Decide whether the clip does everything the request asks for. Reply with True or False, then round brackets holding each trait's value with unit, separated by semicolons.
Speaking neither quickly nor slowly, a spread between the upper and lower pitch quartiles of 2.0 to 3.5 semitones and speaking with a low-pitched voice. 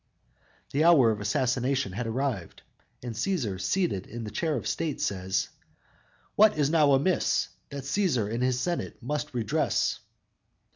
False (150 wpm; 5.4 semitones; 130 Hz)